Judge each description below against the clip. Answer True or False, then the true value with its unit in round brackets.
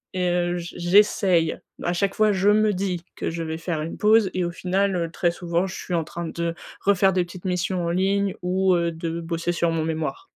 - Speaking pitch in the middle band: True (175 Hz)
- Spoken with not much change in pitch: True (2.2 semitones)